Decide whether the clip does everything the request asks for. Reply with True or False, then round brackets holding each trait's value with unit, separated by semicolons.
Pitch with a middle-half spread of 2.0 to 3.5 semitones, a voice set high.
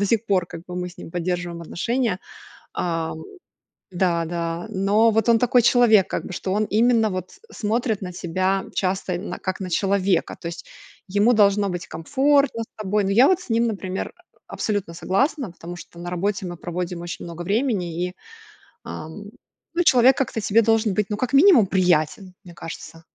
False (4.2 semitones; 195 Hz)